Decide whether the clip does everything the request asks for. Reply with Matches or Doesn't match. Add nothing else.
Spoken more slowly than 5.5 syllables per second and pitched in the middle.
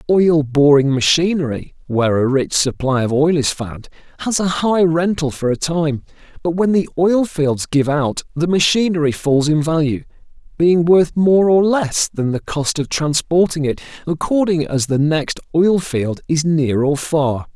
Matches